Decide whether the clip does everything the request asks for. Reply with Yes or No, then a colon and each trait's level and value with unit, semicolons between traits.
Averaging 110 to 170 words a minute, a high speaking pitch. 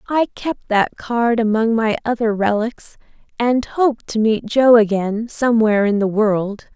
Yes: average, 160 wpm; high, 225 Hz